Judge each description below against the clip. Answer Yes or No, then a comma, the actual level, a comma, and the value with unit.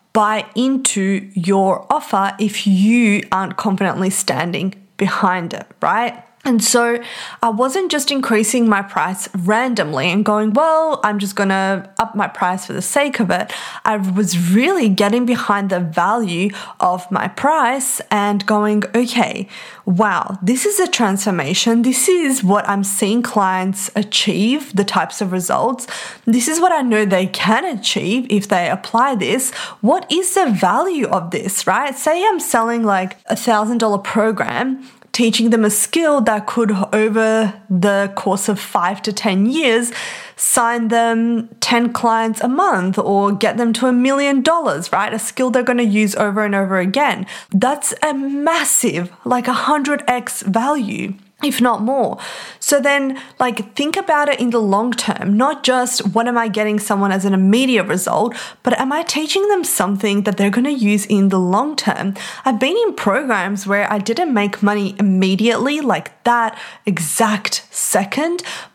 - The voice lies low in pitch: No, high, 220 Hz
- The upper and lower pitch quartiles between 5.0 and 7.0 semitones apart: No, average, 4.0 semitones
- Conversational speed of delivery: Yes, average, 165 wpm